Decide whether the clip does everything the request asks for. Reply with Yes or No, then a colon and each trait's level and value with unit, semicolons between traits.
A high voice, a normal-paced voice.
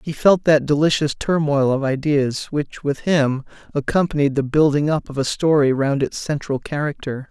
No: medium, 145 Hz; average, 175 wpm